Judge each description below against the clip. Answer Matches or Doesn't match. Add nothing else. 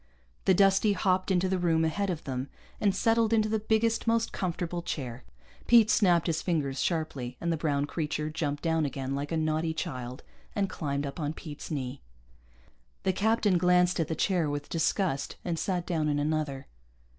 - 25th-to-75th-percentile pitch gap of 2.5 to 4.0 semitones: Doesn't match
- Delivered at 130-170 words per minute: Doesn't match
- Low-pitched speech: Doesn't match